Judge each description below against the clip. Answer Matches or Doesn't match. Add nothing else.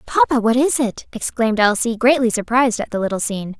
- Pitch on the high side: Matches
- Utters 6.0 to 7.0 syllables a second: Matches